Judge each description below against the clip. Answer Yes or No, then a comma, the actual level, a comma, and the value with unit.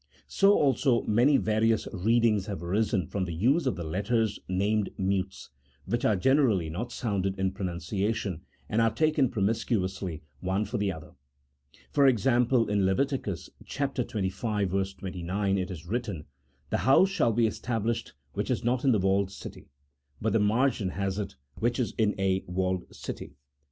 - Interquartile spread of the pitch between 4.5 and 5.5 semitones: No, average, 3.9 semitones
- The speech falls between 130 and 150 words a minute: No, average, 160 wpm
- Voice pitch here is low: Yes, low, 105 Hz